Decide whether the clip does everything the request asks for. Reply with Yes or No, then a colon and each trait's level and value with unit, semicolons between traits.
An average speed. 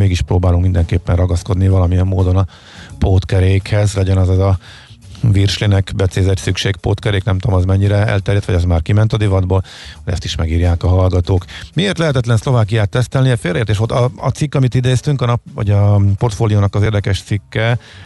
No: fast, 175 wpm